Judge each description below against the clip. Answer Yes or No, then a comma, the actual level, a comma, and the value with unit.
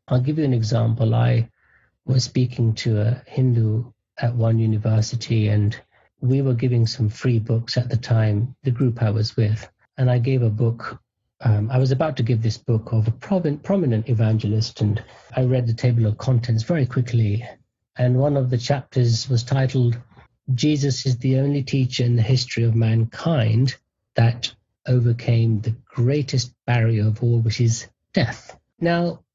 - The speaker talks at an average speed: Yes, average, 170 wpm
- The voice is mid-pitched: No, low, 120 Hz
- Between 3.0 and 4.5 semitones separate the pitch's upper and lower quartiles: No, narrow, 2.4 semitones